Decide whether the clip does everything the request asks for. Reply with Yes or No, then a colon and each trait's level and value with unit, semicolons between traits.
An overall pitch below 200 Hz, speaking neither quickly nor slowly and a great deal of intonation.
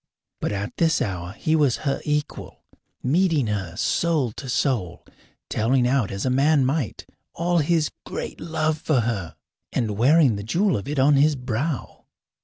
Yes: low, 135 Hz; average, 165 wpm; wide, 6.0 semitones